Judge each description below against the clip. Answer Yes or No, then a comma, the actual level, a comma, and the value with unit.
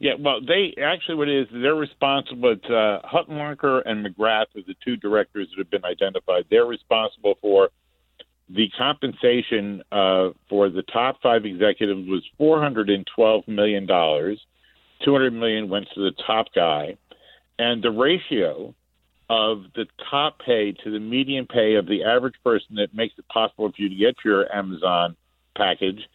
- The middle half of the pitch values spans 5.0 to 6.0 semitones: Yes, wide, 5.5 semitones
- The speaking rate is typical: Yes, average, 170 wpm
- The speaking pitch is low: Yes, low, 110 Hz